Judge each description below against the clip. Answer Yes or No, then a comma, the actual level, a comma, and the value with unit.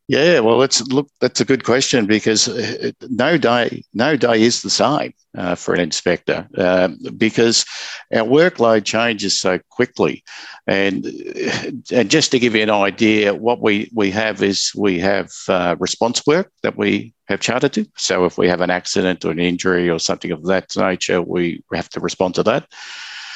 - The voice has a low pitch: Yes, low, 110 Hz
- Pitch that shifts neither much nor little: Yes, average, 3.6 semitones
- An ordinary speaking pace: Yes, average, 180 wpm